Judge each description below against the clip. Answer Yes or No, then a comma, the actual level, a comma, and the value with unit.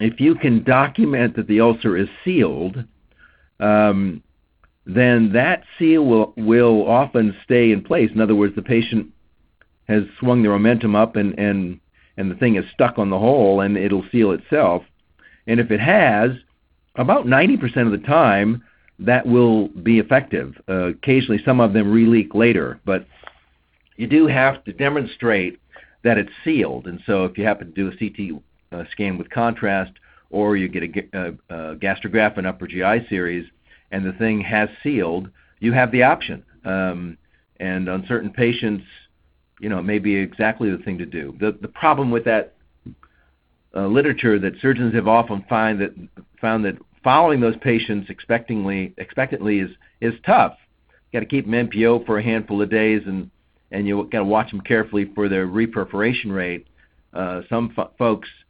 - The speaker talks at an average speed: Yes, average, 175 wpm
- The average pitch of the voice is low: Yes, low, 105 Hz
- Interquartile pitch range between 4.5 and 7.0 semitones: No, average, 3.5 semitones